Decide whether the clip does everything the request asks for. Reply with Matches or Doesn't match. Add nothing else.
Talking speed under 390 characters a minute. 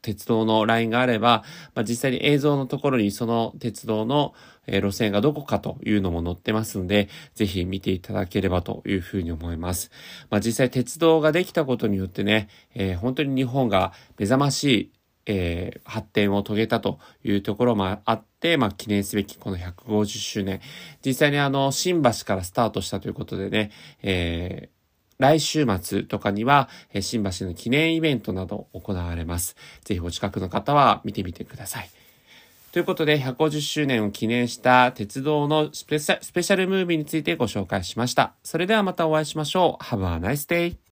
Matches